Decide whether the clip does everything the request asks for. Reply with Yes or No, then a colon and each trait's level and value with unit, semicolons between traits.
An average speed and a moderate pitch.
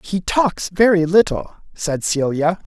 No: slow, 130 wpm; medium, 180 Hz